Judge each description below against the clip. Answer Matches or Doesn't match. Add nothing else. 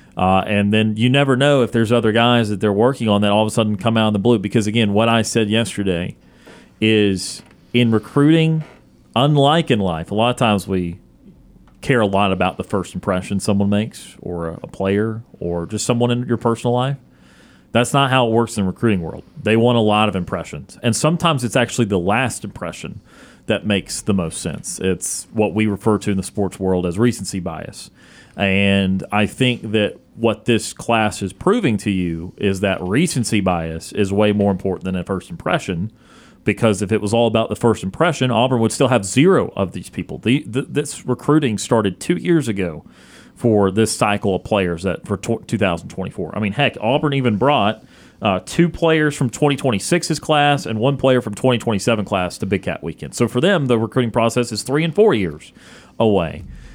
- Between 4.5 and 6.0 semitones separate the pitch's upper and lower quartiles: Doesn't match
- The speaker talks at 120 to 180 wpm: Doesn't match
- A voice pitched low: Matches